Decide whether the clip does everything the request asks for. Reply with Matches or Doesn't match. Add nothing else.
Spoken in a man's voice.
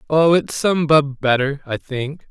Matches